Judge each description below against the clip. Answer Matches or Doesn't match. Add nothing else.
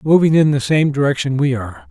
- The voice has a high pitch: Doesn't match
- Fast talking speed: Matches